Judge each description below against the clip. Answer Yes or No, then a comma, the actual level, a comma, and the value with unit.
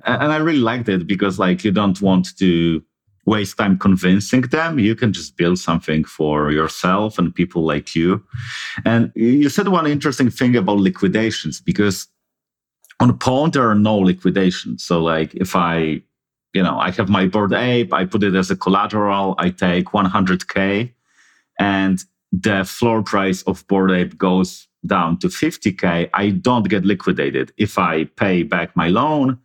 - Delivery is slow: No, average, 175 wpm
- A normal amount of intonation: Yes, average, 3.3 semitones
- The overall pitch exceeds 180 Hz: No, very low, 95 Hz